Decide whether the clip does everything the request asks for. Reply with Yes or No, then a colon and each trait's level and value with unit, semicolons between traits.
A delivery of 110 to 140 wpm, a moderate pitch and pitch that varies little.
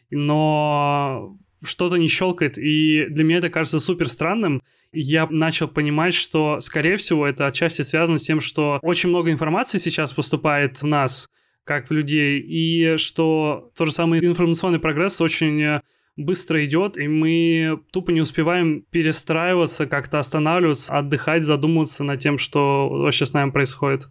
No: average, 150 wpm; medium, 155 Hz; narrow, 2.2 semitones